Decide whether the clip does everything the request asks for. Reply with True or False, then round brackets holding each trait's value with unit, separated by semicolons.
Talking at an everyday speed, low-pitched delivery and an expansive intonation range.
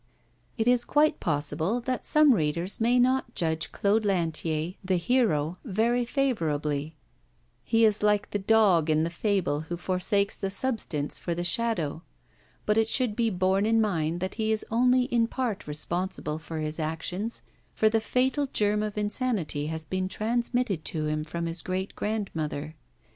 False (165 wpm; 195 Hz; 5.9 semitones)